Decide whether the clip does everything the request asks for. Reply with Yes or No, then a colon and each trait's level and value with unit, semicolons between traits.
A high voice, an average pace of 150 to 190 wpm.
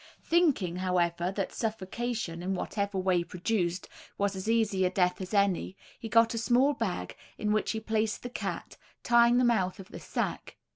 Yes: high, 200 Hz; average, 180 wpm